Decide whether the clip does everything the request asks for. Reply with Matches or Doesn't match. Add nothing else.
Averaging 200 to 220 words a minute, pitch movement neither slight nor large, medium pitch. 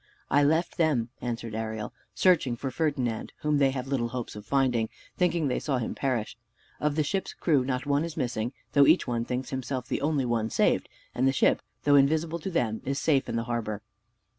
Doesn't match